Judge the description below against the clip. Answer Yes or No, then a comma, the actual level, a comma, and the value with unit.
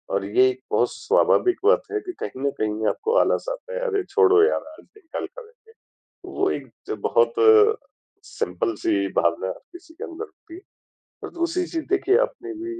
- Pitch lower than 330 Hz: No, very high, 365 Hz